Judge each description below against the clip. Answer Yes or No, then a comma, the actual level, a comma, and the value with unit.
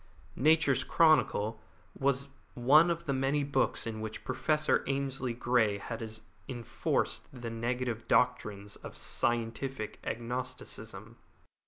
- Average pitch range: Yes, average, 3.1 semitones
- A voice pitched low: Yes, low, 125 Hz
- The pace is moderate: No, slow, 110 wpm